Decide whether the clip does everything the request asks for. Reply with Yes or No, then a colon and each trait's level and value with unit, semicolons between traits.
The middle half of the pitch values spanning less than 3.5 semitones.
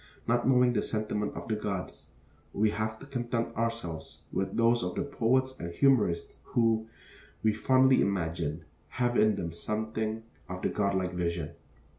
No: average, 4.6 semitones